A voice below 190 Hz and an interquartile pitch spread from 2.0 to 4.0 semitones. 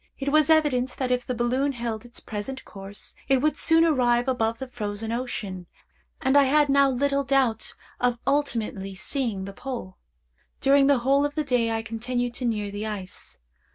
No: very high, 250 Hz; average, 3.7 semitones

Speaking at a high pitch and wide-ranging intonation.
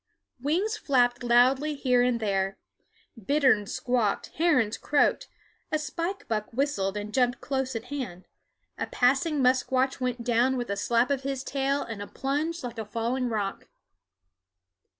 No: very high, 255 Hz; average, 3.5 semitones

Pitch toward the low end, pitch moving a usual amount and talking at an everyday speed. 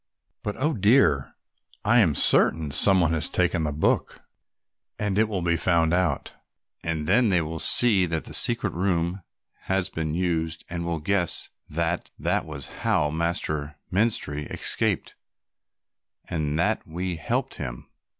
Yes: very low, 85 Hz; average, 3.3 semitones; average, 150 wpm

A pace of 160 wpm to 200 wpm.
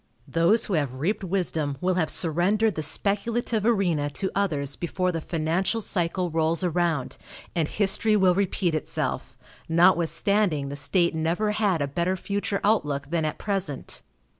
No: average, 150 wpm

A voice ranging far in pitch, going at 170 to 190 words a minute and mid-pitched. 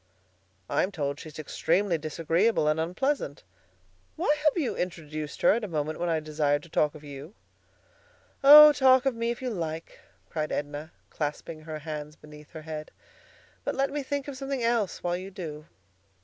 Yes: wide, 7.3 semitones; average, 175 wpm; medium, 165 Hz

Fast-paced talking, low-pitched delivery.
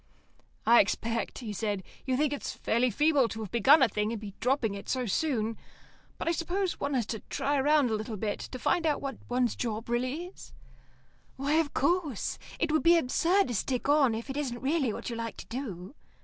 No: fast, 210 wpm; very high, 255 Hz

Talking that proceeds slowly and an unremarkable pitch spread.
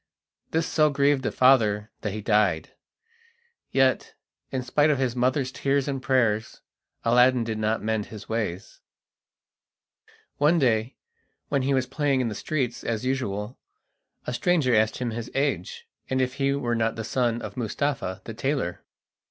No: average, 160 wpm; average, 3.7 semitones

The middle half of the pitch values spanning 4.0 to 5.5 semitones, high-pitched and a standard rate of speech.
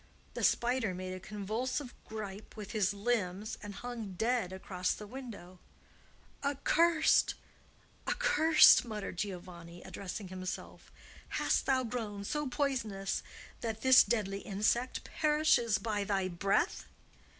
No: average, 4.3 semitones; high, 210 Hz; slow, 115 wpm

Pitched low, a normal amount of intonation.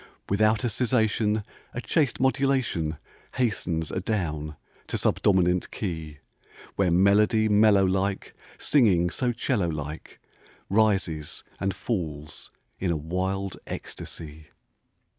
Yes: very low, 95 Hz; average, 4.7 semitones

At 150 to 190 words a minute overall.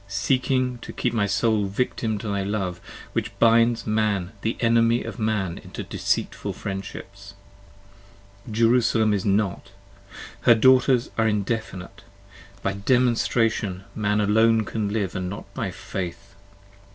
No: slow, 135 wpm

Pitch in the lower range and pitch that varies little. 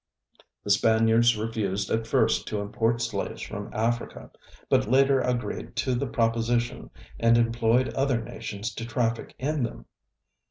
Yes: low, 115 Hz; narrow, 1.4 semitones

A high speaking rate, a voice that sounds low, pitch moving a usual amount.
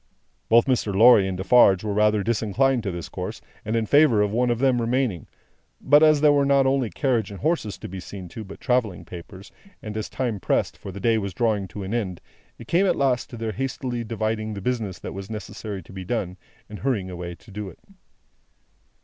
Yes: fast, 220 wpm; low, 110 Hz; average, 4.2 semitones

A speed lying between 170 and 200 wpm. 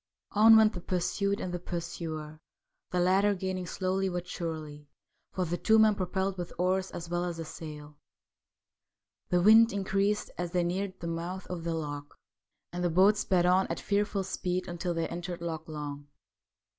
Yes: average, 175 wpm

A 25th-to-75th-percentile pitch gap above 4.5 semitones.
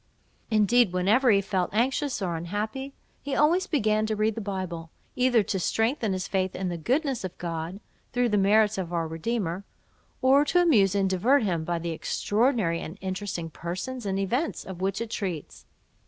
Yes: average, 4.9 semitones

